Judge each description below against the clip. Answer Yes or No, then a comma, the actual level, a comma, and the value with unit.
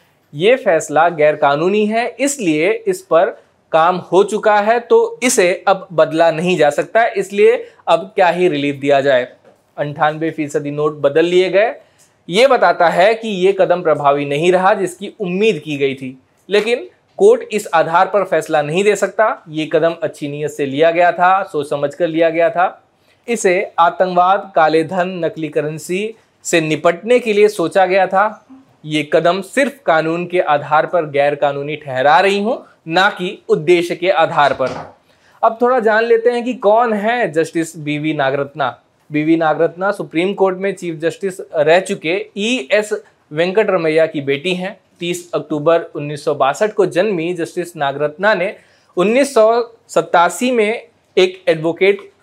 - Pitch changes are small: No, average, 5.1 semitones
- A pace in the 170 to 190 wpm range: No, average, 160 wpm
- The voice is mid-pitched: Yes, medium, 175 Hz